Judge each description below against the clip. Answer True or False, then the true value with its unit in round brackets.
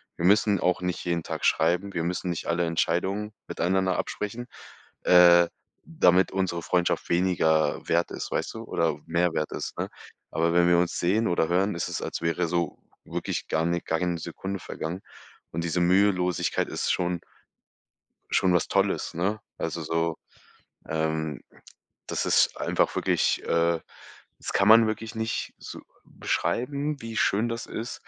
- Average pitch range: True (3.0 semitones)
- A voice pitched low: True (90 Hz)